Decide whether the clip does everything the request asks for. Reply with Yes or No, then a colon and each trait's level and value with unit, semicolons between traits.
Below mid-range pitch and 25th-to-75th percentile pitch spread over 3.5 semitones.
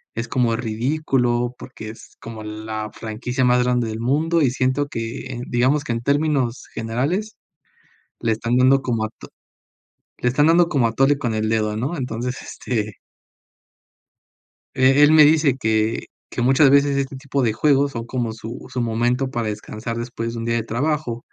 No: low, 125 Hz; average, 3.2 semitones